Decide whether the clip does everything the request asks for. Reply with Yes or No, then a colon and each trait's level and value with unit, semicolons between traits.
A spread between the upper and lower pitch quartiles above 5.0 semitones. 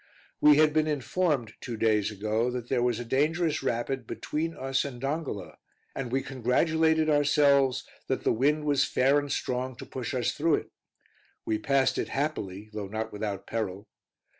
No: average, 4.4 semitones